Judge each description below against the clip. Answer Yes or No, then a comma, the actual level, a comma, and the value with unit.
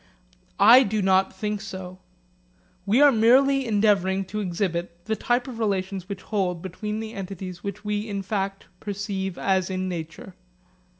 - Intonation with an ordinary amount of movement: No, narrow, 2.3 semitones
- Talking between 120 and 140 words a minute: No, average, 155 wpm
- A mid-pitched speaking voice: No, high, 195 Hz